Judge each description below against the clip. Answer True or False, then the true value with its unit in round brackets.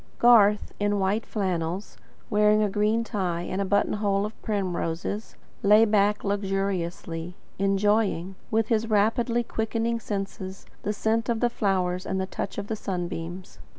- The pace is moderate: True (150 wpm)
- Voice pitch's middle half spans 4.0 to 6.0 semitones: False (2.4 semitones)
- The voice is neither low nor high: False (205 Hz)